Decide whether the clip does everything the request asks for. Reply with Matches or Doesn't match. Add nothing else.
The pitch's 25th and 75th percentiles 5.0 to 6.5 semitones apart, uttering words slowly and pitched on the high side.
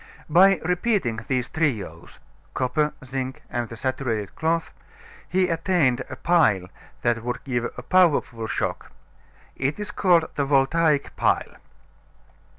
Doesn't match